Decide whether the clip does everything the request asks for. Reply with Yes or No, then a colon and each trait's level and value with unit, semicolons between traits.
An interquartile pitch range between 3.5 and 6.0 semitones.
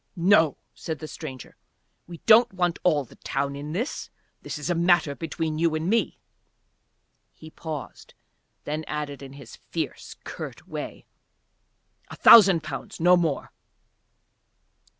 No: average, 3.0 semitones